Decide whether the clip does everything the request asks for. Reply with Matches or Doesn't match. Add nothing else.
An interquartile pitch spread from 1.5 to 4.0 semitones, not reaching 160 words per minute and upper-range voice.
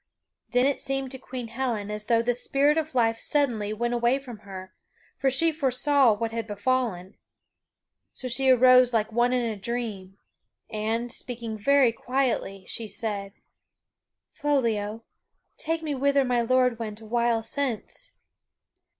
Matches